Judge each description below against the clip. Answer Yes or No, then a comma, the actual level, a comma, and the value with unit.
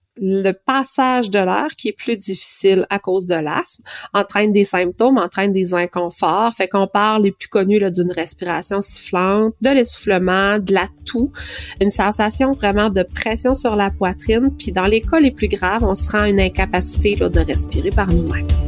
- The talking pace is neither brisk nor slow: Yes, average, 190 wpm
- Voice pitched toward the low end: No, high, 200 Hz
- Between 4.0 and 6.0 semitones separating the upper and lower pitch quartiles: No, average, 3.4 semitones